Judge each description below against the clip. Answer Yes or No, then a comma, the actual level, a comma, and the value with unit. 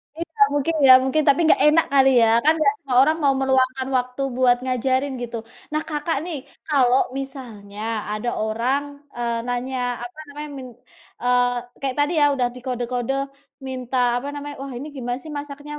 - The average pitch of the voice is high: Yes, very high, 265 Hz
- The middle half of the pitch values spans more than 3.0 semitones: No, average, 2.7 semitones